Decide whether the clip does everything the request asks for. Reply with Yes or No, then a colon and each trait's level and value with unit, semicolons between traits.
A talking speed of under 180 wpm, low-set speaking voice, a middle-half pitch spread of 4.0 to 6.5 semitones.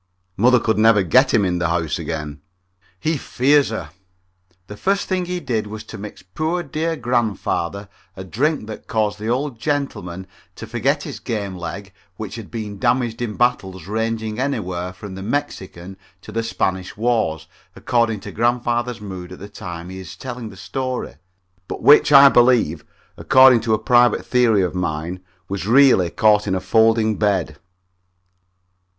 Yes: average, 165 wpm; low, 110 Hz; average, 4.6 semitones